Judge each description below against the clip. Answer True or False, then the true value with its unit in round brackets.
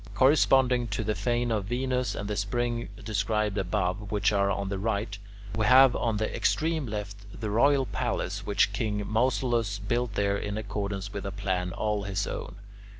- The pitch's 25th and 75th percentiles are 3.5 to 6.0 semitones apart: False (3.1 semitones)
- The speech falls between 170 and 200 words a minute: True (175 wpm)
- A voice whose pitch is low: True (105 Hz)